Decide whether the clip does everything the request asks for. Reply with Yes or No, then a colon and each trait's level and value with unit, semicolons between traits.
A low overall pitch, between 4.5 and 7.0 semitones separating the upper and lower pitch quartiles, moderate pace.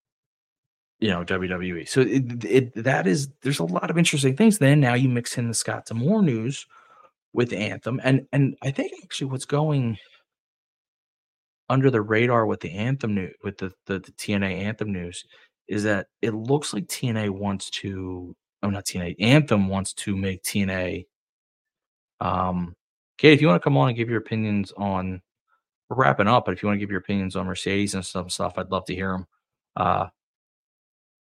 Yes: low, 105 Hz; wide, 5.6 semitones; average, 190 wpm